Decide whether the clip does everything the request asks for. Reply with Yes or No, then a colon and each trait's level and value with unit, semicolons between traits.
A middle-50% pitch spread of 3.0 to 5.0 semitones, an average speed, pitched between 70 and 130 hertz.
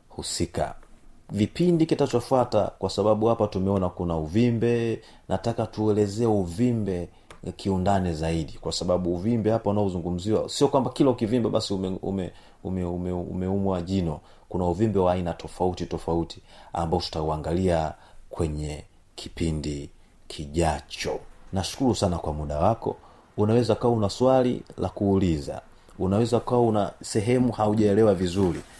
Yes: average, 4.4 semitones; average, 115 wpm; very low, 95 Hz